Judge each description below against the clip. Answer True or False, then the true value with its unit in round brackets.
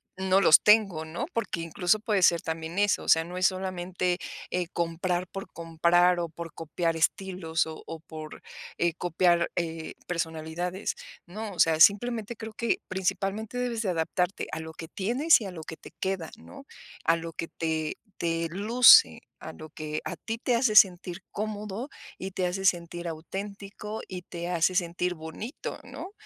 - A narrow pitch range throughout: False (3.3 semitones)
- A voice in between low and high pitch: True (180 Hz)